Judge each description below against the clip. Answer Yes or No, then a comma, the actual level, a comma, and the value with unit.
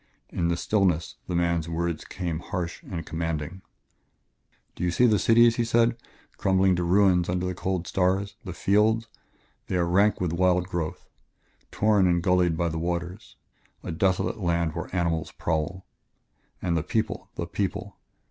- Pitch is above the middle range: No, very low, 90 Hz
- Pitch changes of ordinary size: No, narrow, 2.2 semitones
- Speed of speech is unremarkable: Yes, average, 160 wpm